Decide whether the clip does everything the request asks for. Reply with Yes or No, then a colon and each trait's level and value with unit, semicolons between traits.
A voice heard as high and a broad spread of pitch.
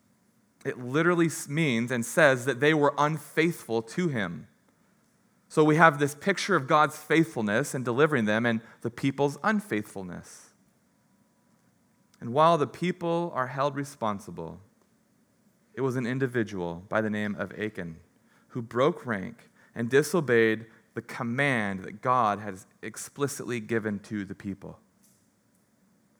No: low, 130 Hz; wide, 5.9 semitones